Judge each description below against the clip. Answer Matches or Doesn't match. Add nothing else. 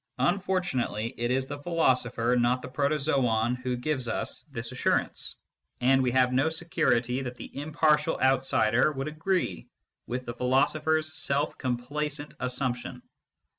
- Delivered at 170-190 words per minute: Doesn't match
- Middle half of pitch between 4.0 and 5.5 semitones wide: Doesn't match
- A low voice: Matches